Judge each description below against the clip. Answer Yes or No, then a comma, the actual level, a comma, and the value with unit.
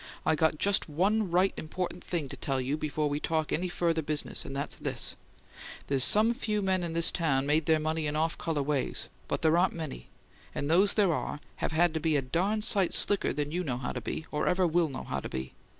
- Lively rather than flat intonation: No, average, 3.5 semitones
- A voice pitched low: No, medium, 160 Hz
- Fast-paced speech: Yes, fast, 235 wpm